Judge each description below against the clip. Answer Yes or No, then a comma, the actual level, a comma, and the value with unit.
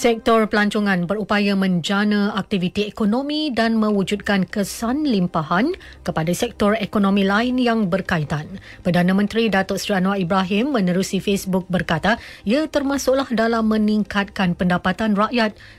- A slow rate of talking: Yes, slow, 120 wpm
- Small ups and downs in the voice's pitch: No, average, 3.0 semitones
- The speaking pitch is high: Yes, high, 205 Hz